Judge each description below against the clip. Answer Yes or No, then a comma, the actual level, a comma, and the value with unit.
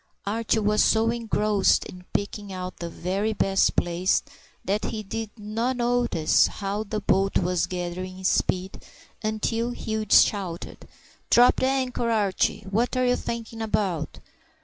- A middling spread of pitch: Yes, average, 3.3 semitones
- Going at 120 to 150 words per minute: Yes, average, 140 wpm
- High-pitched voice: Yes, high, 210 Hz